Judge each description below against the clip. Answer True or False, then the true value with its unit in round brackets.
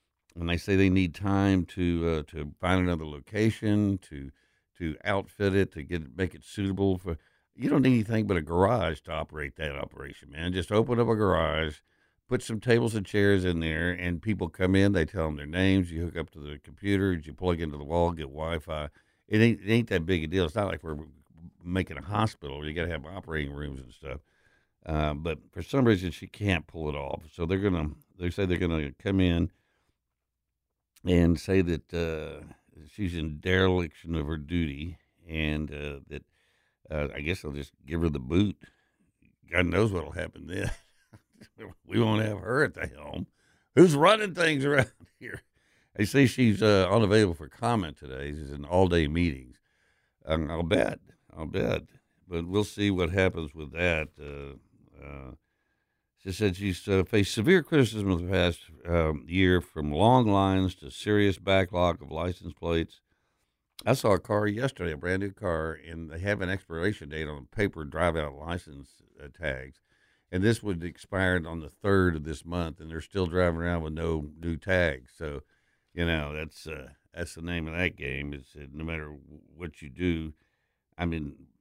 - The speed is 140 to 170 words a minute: False (190 wpm)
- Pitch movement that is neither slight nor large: True (3.9 semitones)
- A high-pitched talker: False (85 Hz)